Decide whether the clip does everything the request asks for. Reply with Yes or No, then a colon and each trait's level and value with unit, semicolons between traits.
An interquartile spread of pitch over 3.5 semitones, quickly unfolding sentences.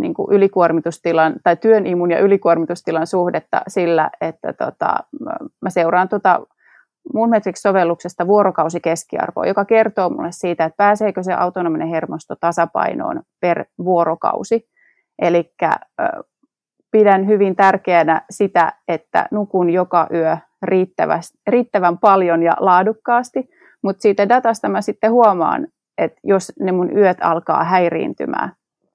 No: average, 4.3 semitones; average, 115 wpm